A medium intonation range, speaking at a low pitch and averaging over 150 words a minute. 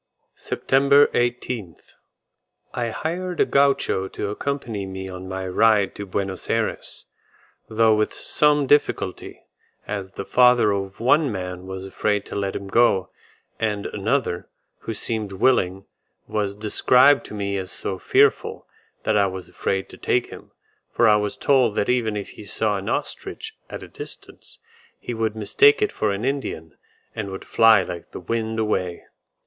Yes: average, 4.0 semitones; low, 105 Hz; average, 160 wpm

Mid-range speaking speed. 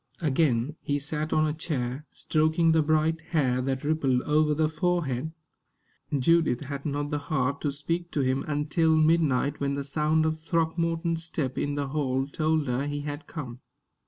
Yes: average, 170 wpm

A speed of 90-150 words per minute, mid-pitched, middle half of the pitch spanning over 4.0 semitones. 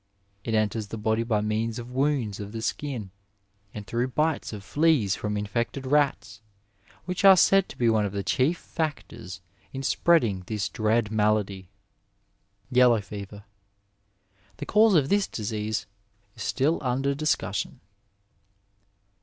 No: average, 145 wpm; low, 115 Hz; average, 5.0 semitones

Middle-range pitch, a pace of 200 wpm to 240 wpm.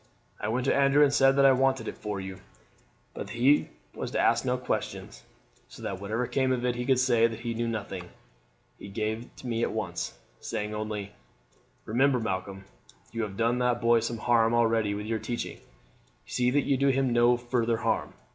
No: low, 120 Hz; fast, 205 wpm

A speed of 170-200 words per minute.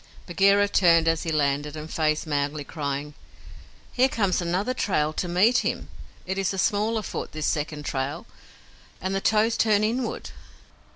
No: average, 160 wpm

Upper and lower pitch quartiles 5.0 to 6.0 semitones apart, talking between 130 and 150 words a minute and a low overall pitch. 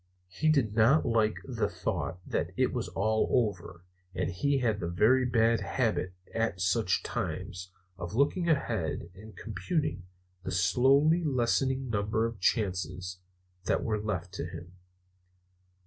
Yes: wide, 5.4 semitones; average, 140 wpm; low, 110 Hz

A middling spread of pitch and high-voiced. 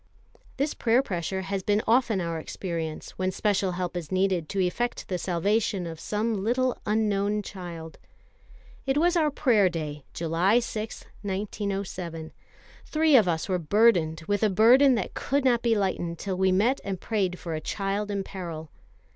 Yes: average, 4.0 semitones; high, 195 Hz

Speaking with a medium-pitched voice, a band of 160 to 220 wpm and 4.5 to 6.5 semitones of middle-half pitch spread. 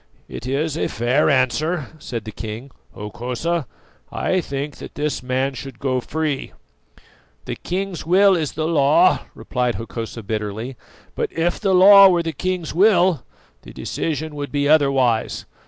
No: medium, 145 Hz; average, 150 wpm; average, 5.2 semitones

